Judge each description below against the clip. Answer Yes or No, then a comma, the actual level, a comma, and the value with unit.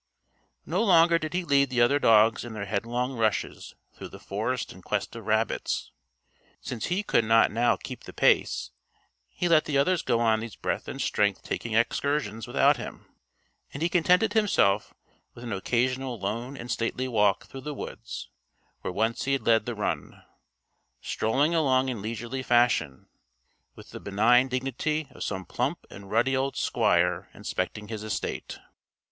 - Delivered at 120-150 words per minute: No, average, 165 wpm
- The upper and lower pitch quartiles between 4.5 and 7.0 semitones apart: No, average, 4.1 semitones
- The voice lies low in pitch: Yes, low, 120 Hz